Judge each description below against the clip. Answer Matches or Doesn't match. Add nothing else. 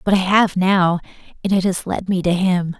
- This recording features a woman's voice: Matches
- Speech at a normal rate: Doesn't match